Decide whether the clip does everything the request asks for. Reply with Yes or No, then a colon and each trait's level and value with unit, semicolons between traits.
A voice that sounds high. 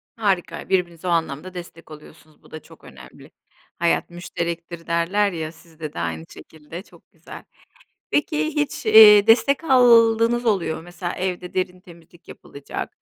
No: medium, 175 Hz